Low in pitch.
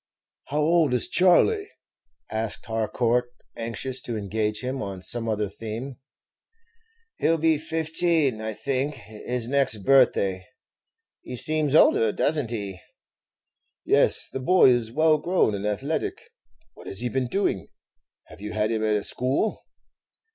Yes: low, 125 Hz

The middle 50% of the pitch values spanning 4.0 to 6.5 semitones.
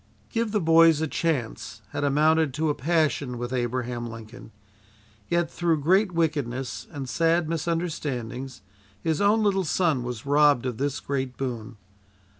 Yes: average, 4.9 semitones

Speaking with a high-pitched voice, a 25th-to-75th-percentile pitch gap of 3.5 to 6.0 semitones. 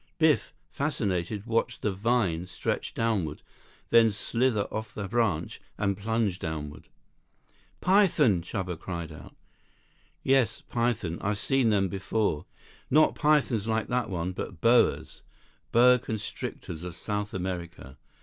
No: low, 105 Hz; average, 4.8 semitones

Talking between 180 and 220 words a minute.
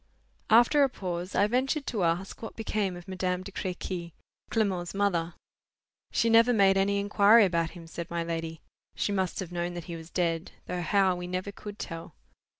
Yes: average, 185 wpm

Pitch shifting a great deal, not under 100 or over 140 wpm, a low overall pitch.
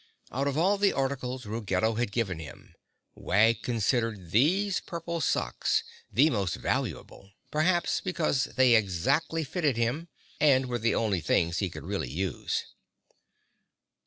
Yes: wide, 7.3 semitones; slow, 135 wpm; low, 120 Hz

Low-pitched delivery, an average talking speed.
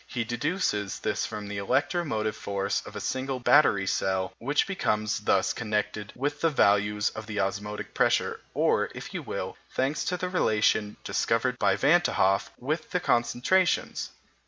Yes: low, 110 Hz; average, 160 wpm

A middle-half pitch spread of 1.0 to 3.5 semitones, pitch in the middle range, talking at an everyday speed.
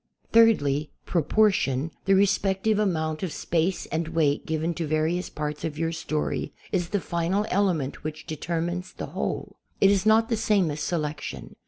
No: average, 3.9 semitones; medium, 170 Hz; average, 160 wpm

